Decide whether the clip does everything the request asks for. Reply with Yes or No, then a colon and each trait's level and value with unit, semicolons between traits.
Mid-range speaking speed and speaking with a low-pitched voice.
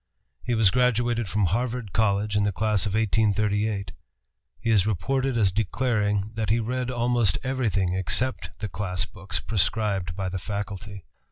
Yes: average, 155 wpm; low, 105 Hz